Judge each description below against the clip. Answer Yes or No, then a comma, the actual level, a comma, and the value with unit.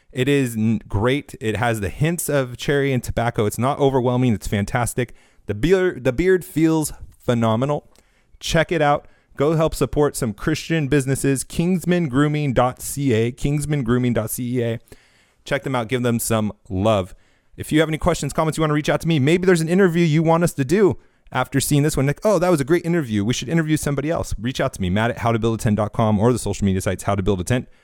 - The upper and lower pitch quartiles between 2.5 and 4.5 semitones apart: No, average, 5.3 semitones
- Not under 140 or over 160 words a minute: No, fast, 205 wpm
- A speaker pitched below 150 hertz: Yes, low, 135 Hz